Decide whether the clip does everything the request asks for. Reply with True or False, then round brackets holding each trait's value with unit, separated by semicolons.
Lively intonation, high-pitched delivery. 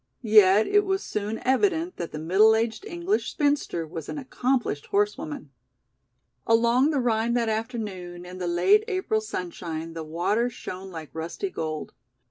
True (6.8 semitones; 220 Hz)